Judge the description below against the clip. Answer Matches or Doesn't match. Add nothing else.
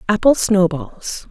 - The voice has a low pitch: Doesn't match